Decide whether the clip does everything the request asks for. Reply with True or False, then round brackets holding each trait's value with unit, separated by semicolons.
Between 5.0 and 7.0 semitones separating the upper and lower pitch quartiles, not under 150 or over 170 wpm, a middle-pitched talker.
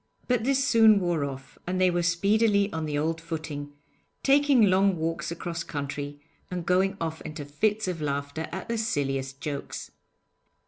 True (5.3 semitones; 165 wpm; 170 Hz)